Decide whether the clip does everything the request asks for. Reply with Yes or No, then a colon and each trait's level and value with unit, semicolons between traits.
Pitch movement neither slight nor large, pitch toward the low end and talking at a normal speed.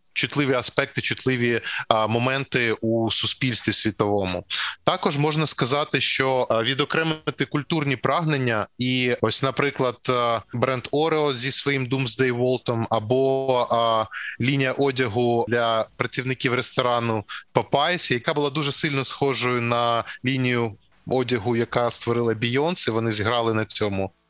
Yes: average, 3.0 semitones; low, 125 Hz; average, 125 wpm